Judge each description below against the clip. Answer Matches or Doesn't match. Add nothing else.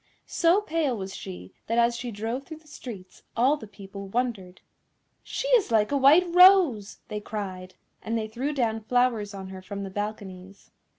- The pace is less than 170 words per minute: Doesn't match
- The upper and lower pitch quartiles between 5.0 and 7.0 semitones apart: Matches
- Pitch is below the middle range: Doesn't match